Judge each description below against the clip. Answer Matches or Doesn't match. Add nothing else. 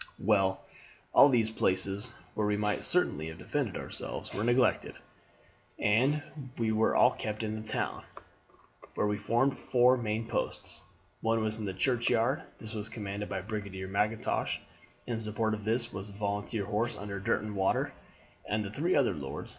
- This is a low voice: Matches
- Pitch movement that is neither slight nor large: Doesn't match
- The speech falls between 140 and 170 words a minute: Matches